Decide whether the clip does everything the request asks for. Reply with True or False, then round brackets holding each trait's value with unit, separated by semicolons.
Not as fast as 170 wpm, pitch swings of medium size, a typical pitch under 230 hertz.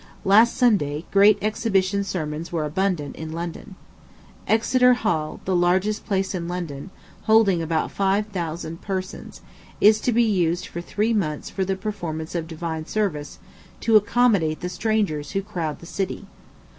True (150 wpm; 4.4 semitones; 185 Hz)